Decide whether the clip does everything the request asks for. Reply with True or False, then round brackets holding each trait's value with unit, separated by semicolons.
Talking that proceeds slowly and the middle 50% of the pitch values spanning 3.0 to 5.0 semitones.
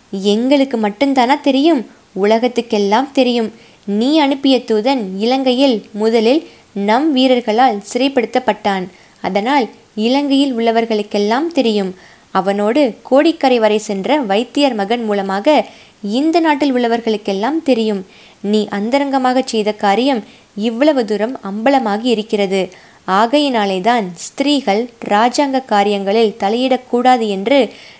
False (90 wpm; 4.3 semitones)